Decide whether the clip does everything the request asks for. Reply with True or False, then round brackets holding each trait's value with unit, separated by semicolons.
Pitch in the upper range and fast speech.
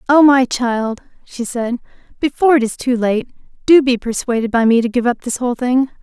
True (245 Hz; 210 wpm)